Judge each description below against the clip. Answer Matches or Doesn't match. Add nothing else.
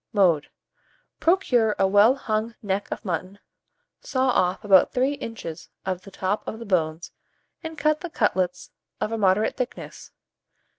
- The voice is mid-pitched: Doesn't match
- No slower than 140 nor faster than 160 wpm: Matches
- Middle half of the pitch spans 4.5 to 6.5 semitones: Matches